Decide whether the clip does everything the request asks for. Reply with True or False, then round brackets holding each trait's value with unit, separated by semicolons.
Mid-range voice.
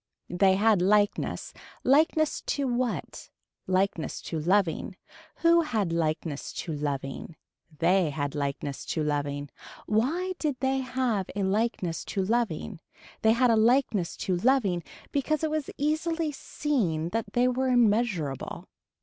False (210 Hz)